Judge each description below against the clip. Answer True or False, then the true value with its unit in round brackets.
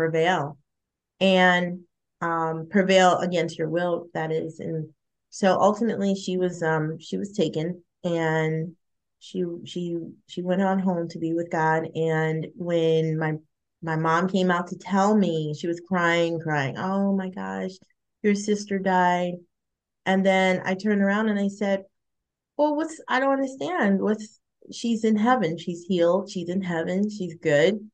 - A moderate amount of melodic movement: True (3.2 semitones)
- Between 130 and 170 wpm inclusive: True (155 wpm)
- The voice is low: False (175 Hz)